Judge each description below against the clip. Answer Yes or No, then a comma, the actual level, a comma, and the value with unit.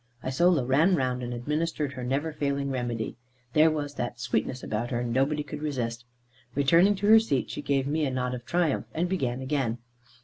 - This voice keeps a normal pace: Yes, average, 195 wpm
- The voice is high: No, low, 135 Hz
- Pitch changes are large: No, average, 3.7 semitones